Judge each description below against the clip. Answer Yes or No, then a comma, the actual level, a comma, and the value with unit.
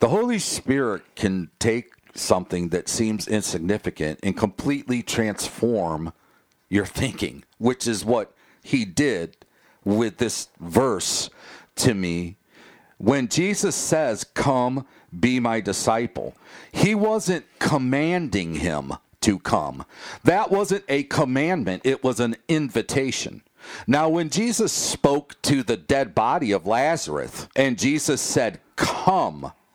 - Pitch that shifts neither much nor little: No, wide, 6.2 semitones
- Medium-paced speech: No, slow, 120 wpm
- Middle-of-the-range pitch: No, low, 125 Hz